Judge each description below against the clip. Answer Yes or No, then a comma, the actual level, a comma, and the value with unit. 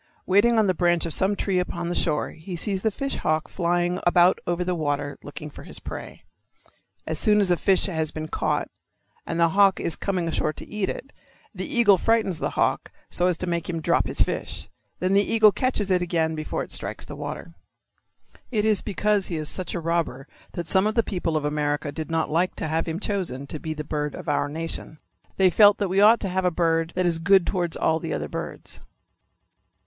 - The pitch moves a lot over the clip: No, average, 3.5 semitones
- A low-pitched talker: No, medium, 175 Hz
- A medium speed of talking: No, fast, 225 wpm